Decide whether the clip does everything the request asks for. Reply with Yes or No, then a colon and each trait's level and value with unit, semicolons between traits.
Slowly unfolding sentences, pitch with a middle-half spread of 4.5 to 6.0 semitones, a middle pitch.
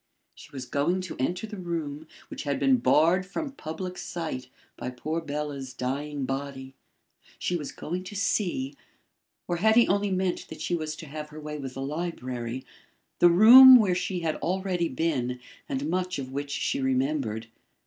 No: average, 175 wpm; average, 5.0 semitones; medium, 155 Hz